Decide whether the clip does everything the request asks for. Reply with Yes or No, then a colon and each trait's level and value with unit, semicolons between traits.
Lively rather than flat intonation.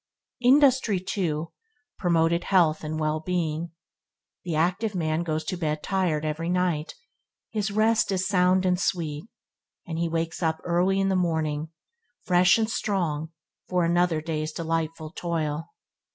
No: average, 2.7 semitones